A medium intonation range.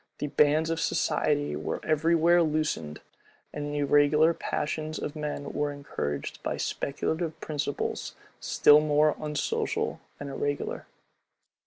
No: narrow, 1.5 semitones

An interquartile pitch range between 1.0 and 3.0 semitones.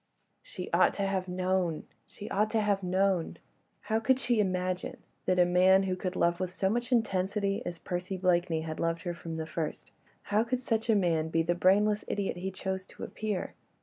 Yes: average, 2.7 semitones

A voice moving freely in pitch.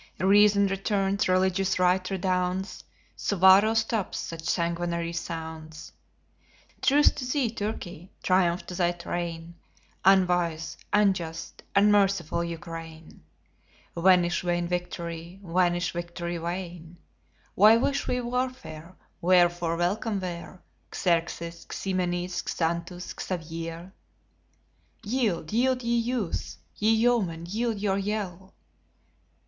No: average, 2.9 semitones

